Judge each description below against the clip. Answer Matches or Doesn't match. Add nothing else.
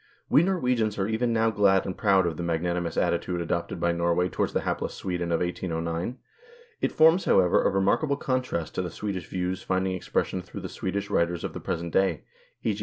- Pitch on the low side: Matches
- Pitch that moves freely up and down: Doesn't match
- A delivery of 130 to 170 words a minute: Doesn't match